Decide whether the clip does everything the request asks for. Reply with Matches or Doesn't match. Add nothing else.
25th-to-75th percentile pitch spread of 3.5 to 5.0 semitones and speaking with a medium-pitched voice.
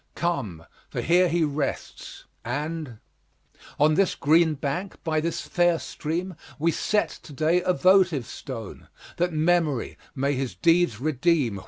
Matches